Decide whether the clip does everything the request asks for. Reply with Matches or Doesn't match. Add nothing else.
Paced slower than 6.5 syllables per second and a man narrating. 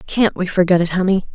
Doesn't match